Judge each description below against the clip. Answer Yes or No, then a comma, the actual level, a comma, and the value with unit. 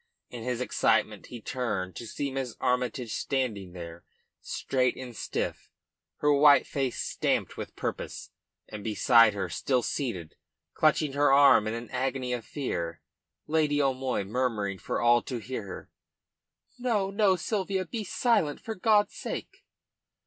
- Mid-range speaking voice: No, low, 130 Hz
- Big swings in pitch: No, average, 4.7 semitones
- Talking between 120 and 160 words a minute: Yes, average, 145 wpm